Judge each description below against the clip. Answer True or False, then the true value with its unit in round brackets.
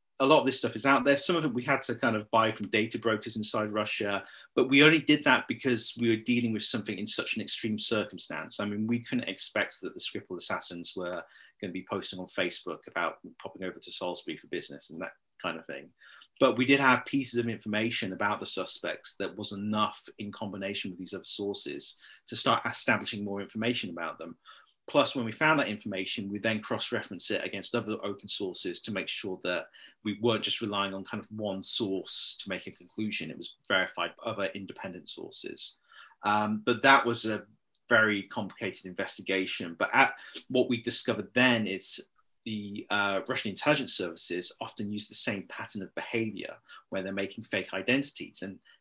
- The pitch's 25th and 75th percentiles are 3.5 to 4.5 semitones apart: False (2.9 semitones)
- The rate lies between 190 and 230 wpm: True (200 wpm)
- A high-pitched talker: False (110 Hz)